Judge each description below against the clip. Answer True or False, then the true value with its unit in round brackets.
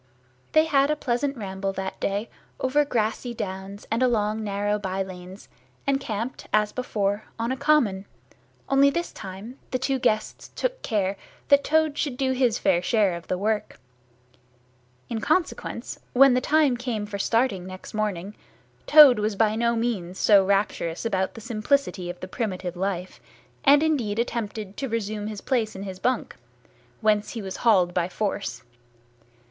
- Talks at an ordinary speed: True (160 wpm)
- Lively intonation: False (4.7 semitones)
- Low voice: False (215 Hz)